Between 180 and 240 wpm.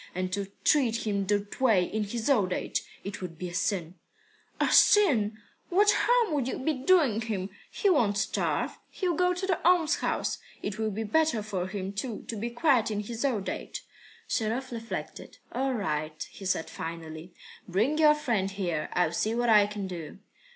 Yes: average, 185 wpm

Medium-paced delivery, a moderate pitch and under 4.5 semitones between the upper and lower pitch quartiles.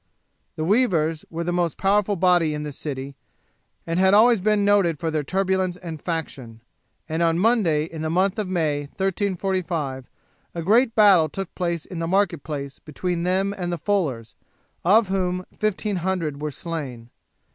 Yes: average, 170 wpm; medium, 175 Hz; average, 3.7 semitones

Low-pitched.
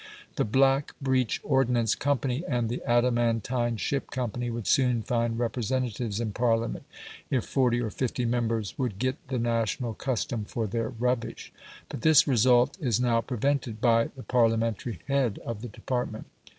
Yes: low, 120 Hz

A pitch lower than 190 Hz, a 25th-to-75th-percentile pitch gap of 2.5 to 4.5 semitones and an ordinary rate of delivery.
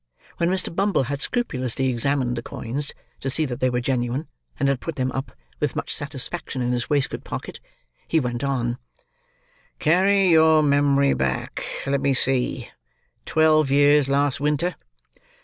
Yes: medium, 140 Hz; average, 3.4 semitones; average, 150 wpm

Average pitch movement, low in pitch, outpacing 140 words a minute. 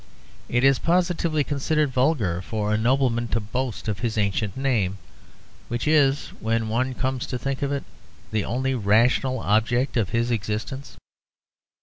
Yes: average, 3.7 semitones; low, 120 Hz; average, 150 wpm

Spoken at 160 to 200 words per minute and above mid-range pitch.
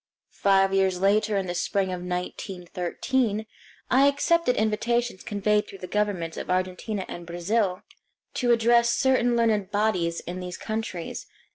No: average, 140 wpm; high, 200 Hz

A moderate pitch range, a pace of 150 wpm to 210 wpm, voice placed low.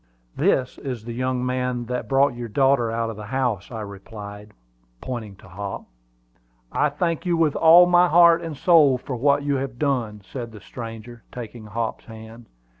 Yes: average, 3.9 semitones; average, 180 wpm; low, 125 Hz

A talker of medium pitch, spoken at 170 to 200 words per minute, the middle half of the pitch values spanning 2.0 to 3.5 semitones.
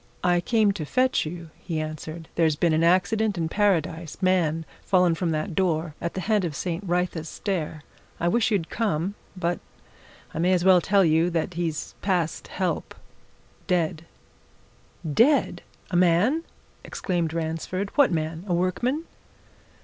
No: medium, 175 Hz; average, 150 wpm; average, 2.8 semitones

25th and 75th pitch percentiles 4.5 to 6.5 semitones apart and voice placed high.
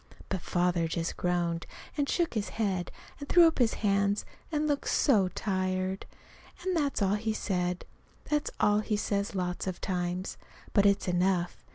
No: average, 3.7 semitones; high, 195 Hz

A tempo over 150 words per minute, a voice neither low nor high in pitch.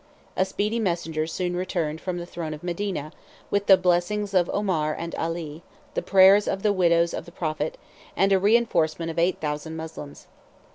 Yes: average, 180 wpm; medium, 175 Hz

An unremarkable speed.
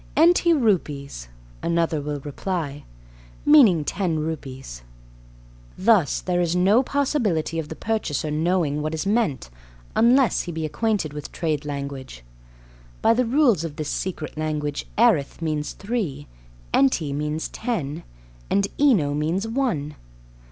No: slow, 130 wpm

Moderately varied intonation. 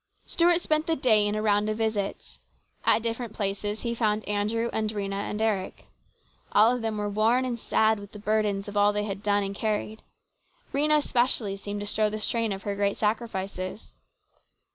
No: narrow, 1.9 semitones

